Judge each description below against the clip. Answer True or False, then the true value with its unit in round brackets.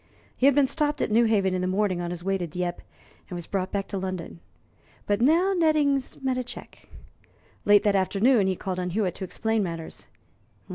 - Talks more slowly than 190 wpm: False (200 wpm)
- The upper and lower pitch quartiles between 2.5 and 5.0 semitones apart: False (5.6 semitones)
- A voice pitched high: True (200 Hz)